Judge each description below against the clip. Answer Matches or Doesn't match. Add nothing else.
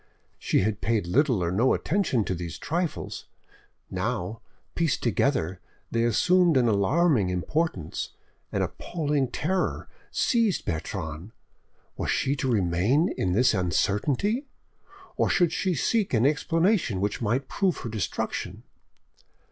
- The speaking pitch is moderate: Doesn't match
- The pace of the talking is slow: Matches